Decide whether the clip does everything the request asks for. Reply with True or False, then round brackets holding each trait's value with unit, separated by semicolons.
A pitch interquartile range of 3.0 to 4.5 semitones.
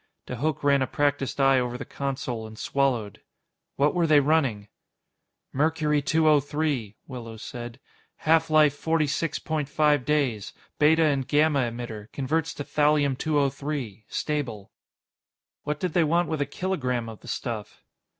True (3.7 semitones)